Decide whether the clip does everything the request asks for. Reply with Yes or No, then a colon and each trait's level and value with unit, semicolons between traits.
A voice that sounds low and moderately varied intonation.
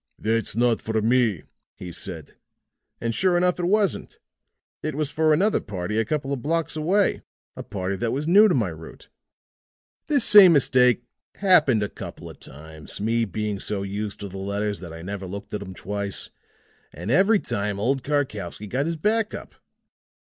No: low, 115 Hz; wide, 7.6 semitones